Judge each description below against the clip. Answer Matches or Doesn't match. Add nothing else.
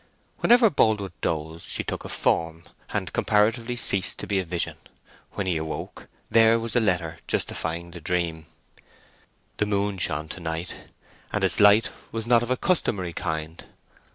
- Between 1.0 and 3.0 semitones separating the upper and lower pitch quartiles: Doesn't match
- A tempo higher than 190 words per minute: Doesn't match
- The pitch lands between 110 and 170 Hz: Doesn't match